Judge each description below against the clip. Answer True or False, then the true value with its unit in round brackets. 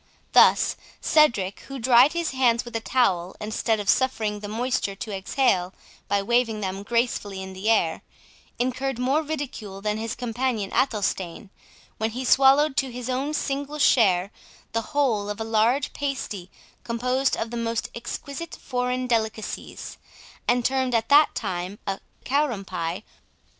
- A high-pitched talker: True (235 Hz)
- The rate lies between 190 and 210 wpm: False (150 wpm)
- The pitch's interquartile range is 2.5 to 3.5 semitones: False (4.2 semitones)